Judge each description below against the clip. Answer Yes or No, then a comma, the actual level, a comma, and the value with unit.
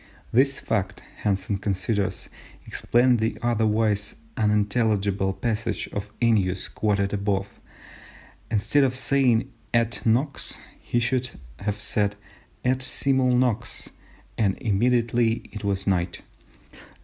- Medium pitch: No, low, 110 Hz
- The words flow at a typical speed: No, slow, 105 wpm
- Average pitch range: Yes, average, 3.2 semitones